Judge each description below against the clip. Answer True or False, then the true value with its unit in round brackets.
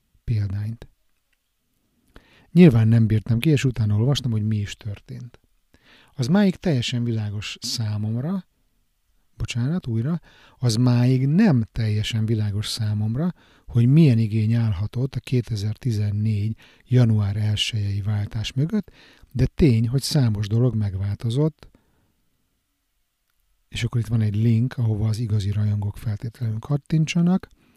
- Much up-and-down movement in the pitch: False (3.3 semitones)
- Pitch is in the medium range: False (115 Hz)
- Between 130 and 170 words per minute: False (115 wpm)